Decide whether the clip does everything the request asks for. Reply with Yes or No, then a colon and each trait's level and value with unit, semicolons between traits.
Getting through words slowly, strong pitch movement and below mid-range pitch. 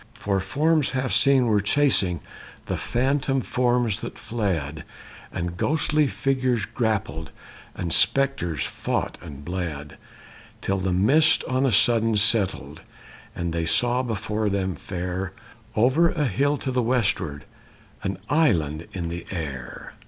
Yes: slow, 130 wpm; wide, 6.8 semitones; low, 105 Hz